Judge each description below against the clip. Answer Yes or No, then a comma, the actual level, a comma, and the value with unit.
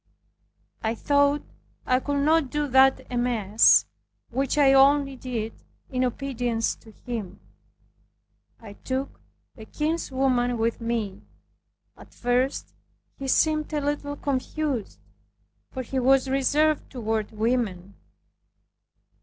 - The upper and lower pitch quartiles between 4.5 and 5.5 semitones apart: No, average, 3.5 semitones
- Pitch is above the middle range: Yes, very high, 260 Hz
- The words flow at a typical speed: No, slow, 110 wpm